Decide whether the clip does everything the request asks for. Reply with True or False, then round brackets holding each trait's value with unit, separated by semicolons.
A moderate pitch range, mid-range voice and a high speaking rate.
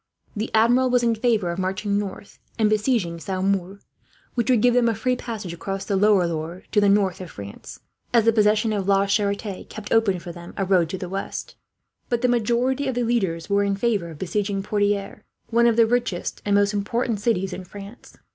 False (3.3 semitones; 205 Hz; 210 wpm)